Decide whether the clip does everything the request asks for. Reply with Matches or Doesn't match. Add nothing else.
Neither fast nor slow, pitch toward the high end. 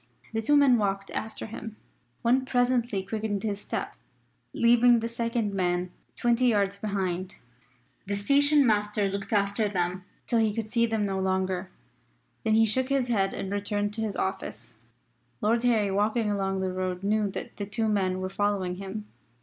Matches